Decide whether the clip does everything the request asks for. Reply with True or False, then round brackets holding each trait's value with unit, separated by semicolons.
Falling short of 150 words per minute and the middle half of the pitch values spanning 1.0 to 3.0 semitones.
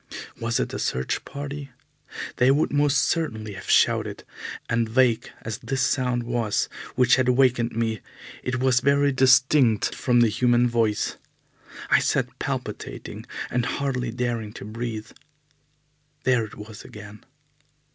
True (135 wpm; 2.7 semitones)